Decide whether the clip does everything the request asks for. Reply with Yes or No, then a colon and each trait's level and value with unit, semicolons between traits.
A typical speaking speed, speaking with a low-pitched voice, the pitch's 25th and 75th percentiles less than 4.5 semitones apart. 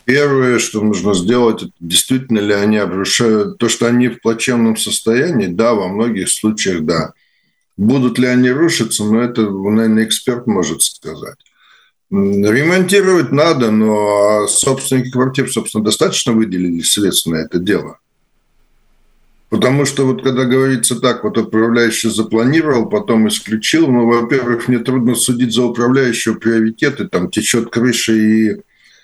Yes: average, 135 wpm; low, 115 Hz; average, 2.7 semitones